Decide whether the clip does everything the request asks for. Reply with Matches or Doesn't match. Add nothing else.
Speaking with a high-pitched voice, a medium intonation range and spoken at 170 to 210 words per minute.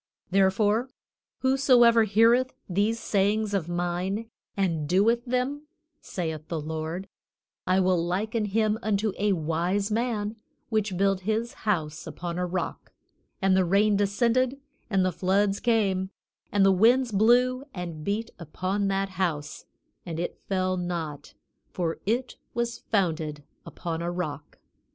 Doesn't match